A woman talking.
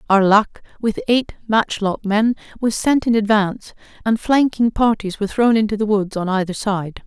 Yes: female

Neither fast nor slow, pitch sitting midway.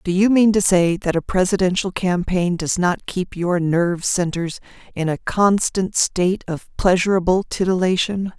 Yes: average, 155 wpm; medium, 180 Hz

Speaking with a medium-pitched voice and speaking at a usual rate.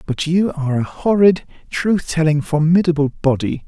Yes: medium, 160 Hz; average, 145 wpm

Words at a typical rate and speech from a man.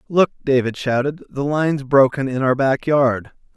Yes: average, 170 wpm; male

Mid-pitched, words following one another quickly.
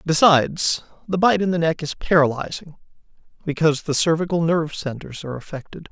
No: medium, 160 Hz; average, 150 wpm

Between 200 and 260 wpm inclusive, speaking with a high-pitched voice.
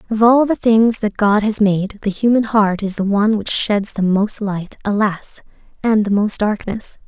Yes: fast, 205 wpm; high, 210 Hz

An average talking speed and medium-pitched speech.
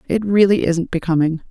Yes: average, 160 wpm; medium, 180 Hz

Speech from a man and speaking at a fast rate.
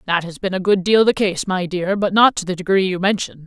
No: female; fast, 295 wpm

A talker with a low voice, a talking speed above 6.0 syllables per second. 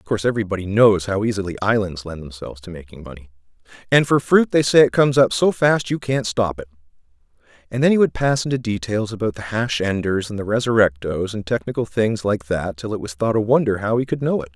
Yes: low, 105 Hz; 6.2 syllables/s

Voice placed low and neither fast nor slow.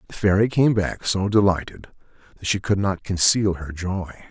Yes: very low, 95 Hz; average, 180 wpm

